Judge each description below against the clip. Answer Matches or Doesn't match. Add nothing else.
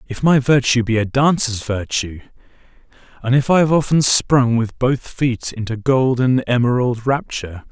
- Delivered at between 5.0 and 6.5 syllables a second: Doesn't match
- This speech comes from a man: Matches